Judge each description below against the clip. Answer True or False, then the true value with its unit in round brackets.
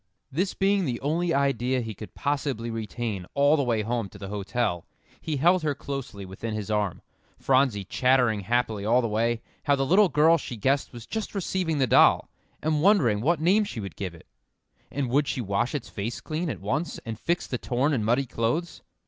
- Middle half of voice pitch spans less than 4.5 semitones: False (5.5 semitones)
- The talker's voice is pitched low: True (130 Hz)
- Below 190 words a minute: False (200 wpm)